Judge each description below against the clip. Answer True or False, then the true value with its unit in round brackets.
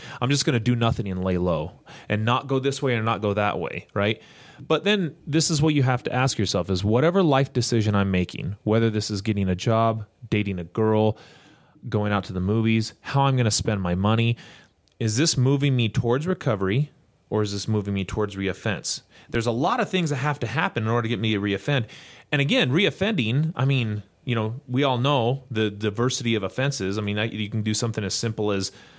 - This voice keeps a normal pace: False (225 wpm)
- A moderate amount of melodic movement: True (4.6 semitones)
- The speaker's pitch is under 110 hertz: False (115 Hz)